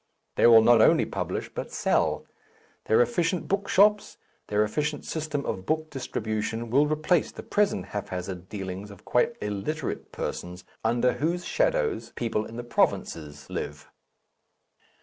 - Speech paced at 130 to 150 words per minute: Yes, average, 140 wpm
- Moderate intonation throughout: No, wide, 7.2 semitones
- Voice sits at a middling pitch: No, low, 120 Hz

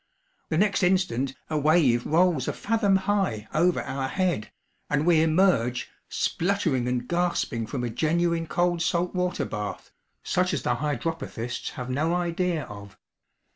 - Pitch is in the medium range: Yes, medium, 160 Hz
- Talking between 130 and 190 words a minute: Yes, average, 145 wpm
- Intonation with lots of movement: Yes, wide, 5.8 semitones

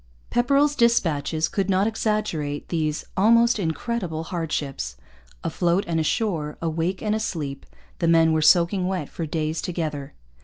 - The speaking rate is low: Yes, slow, 130 wpm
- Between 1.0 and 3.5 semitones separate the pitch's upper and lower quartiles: No, average, 5.0 semitones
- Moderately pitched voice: Yes, medium, 170 Hz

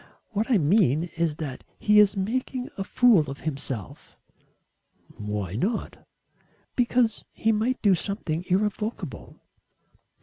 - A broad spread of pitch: Yes, wide, 6.5 semitones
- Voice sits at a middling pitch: No, high, 195 Hz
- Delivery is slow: Yes, slow, 115 wpm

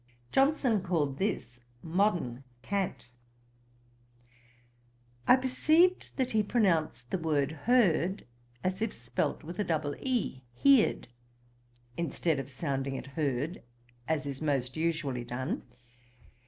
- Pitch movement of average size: No, wide, 7.3 semitones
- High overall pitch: No, medium, 160 Hz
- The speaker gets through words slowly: Yes, slow, 115 wpm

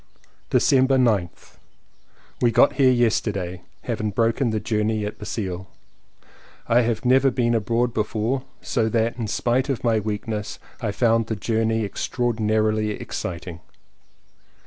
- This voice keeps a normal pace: No, slow, 130 wpm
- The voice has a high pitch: No, low, 110 Hz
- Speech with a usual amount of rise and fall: No, narrow, 2.2 semitones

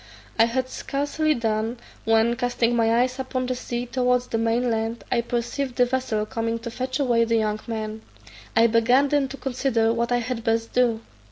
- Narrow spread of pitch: Yes, narrow, 2.0 semitones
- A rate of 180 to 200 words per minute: Yes, average, 190 wpm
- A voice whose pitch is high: Yes, high, 235 Hz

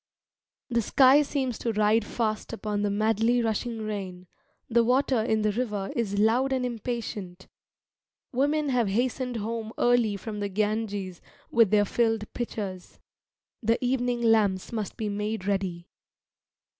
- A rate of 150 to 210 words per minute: No, average, 140 wpm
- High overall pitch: Yes, high, 220 Hz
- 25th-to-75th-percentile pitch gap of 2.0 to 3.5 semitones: Yes, average, 2.8 semitones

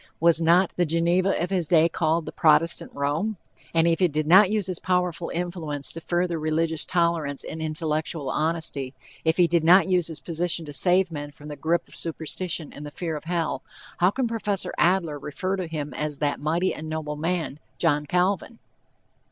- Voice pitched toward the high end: No, medium, 165 Hz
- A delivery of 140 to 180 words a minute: No, average, 195 wpm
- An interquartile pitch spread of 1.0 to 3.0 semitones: Yes, narrow, 2.6 semitones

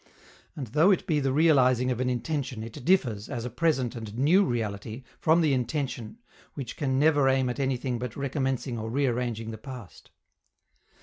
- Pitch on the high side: No, low, 130 Hz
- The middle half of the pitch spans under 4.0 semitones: Yes, average, 3.4 semitones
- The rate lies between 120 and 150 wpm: No, average, 175 wpm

